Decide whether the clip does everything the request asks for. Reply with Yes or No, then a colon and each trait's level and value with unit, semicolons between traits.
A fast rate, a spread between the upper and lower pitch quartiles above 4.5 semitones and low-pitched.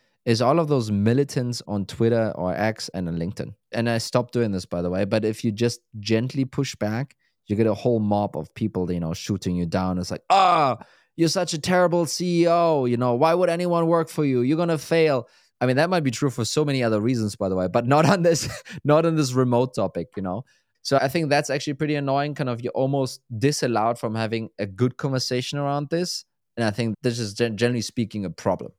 Yes: fast, 230 wpm; average, 5.1 semitones; low, 120 Hz